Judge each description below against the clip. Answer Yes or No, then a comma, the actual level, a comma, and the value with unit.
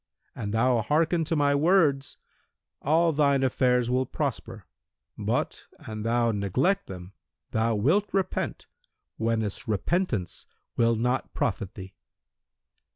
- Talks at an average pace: No, slow, 115 wpm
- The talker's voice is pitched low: Yes, low, 125 Hz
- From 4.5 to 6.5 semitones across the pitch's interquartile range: Yes, wide, 5.4 semitones